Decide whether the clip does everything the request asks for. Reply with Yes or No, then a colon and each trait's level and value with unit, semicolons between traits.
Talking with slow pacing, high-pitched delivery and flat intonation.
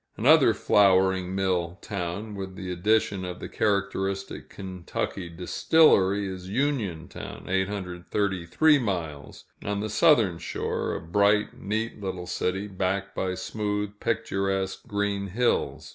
No: slow, 115 wpm; very low, 95 Hz; narrow, 2.1 semitones